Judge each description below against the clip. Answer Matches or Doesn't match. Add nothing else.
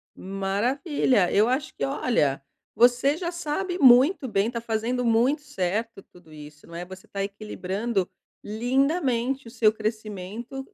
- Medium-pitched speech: Doesn't match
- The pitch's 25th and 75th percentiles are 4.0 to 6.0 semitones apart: Matches